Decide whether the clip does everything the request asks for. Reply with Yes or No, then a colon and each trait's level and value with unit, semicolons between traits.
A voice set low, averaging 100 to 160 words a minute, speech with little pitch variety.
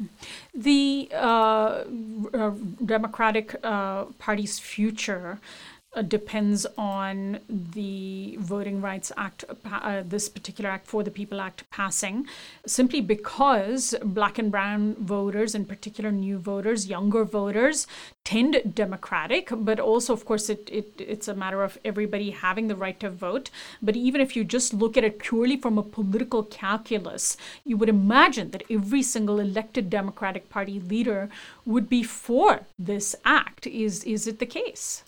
No: high, 215 Hz; average, 150 wpm; narrow, 2.3 semitones